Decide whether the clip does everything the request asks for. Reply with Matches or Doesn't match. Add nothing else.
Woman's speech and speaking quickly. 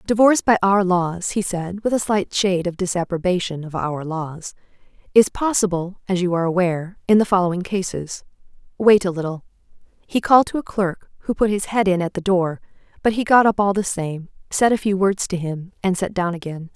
Matches